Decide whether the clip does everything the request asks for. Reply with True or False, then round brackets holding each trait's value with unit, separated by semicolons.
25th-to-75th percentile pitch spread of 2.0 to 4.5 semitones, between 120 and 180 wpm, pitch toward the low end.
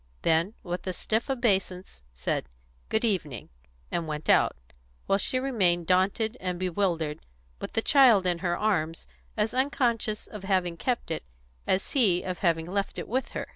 False (4.2 semitones; 170 wpm; 190 Hz)